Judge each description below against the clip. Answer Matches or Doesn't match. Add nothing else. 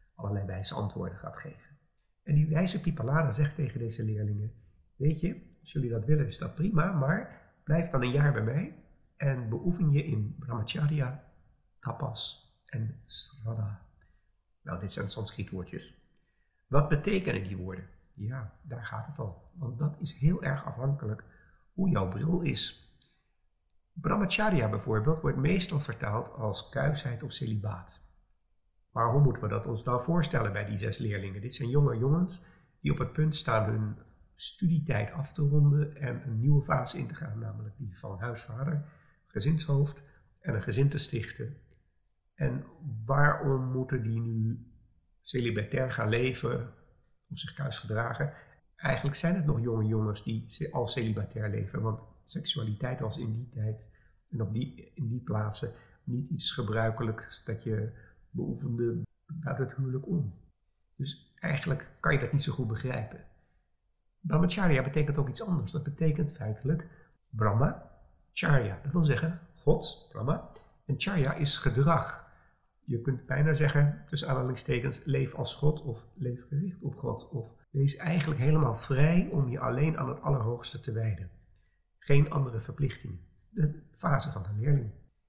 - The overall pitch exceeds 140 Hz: Doesn't match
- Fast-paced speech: Doesn't match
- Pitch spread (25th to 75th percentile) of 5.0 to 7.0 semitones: Matches